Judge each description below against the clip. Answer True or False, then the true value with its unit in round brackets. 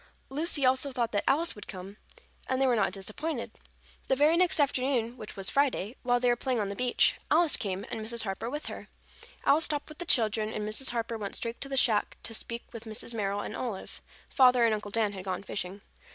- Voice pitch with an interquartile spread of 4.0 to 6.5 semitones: True (4.3 semitones)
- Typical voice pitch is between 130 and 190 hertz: False (235 Hz)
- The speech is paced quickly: True (225 wpm)